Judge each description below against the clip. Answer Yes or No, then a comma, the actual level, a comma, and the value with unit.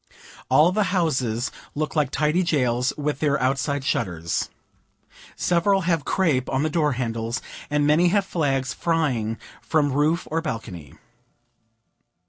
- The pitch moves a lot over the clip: No, average, 4.4 semitones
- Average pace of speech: No, slow, 130 wpm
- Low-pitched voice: No, medium, 145 Hz